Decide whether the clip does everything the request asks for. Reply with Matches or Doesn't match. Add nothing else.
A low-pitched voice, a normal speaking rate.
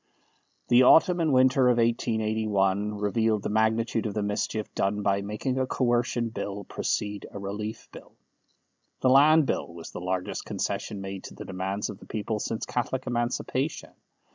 Matches